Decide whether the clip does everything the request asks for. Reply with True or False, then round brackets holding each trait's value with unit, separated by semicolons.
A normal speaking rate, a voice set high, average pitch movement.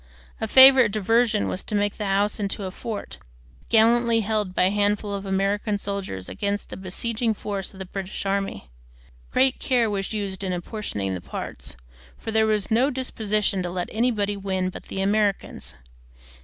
False (170 wpm; 205 Hz; 2.3 semitones)